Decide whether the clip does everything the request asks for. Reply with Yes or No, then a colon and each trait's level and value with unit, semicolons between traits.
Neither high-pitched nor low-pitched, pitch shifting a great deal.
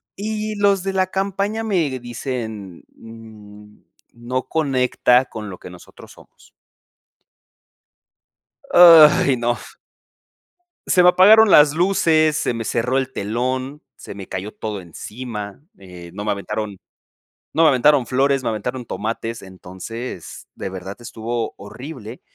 No: low, 125 Hz; wide, 6.5 semitones